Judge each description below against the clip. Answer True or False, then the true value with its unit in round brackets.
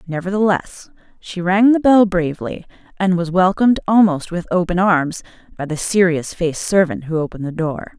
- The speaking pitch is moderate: True (180 Hz)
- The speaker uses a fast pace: False (165 wpm)